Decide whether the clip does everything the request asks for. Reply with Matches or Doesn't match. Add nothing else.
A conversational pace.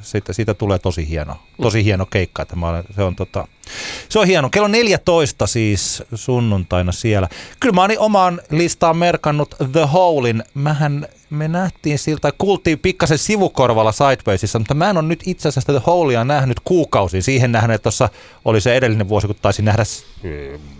Doesn't match